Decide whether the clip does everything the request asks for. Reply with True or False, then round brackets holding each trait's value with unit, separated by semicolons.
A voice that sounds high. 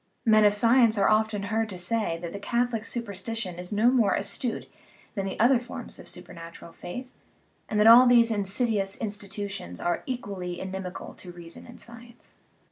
True (210 Hz)